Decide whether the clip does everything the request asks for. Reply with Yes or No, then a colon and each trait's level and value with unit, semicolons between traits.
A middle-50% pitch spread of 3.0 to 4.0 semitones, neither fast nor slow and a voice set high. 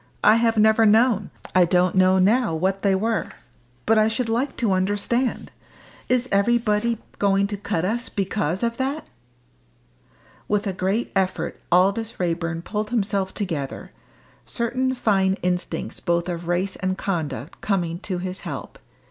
Yes: average, 3.5 semitones; average, 150 wpm; high, 200 Hz